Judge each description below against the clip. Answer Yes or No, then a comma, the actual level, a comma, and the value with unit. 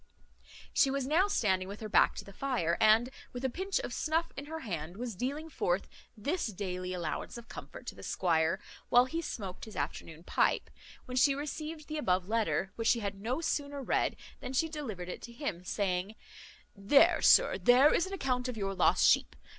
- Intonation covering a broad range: Yes, wide, 7.2 semitones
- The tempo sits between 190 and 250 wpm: Yes, average, 200 wpm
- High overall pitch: Yes, high, 235 Hz